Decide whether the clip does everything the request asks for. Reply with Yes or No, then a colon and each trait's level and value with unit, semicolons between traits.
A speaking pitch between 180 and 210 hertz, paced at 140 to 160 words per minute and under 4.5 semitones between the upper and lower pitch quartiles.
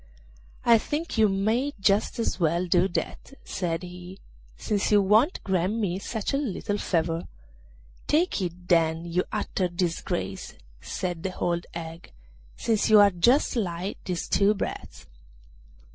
Yes: high, 190 Hz; average, 145 wpm; average, 3.6 semitones